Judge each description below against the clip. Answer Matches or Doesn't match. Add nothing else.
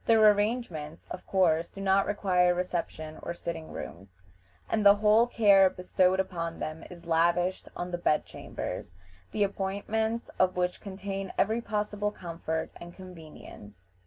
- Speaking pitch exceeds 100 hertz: Matches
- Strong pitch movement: Doesn't match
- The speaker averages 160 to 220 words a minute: Doesn't match